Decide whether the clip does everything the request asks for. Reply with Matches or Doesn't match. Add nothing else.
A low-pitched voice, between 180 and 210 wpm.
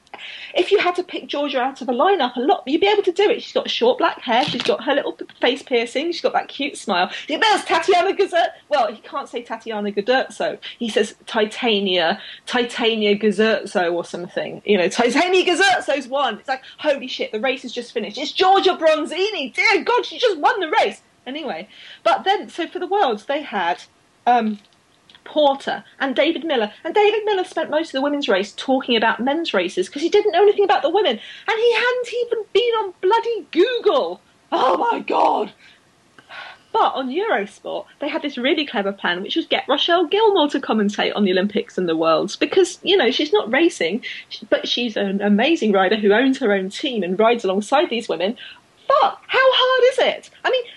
Doesn't match